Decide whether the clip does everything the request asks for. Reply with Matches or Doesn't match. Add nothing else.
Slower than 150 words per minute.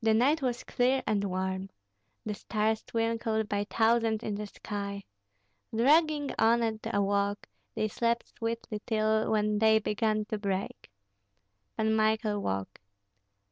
Matches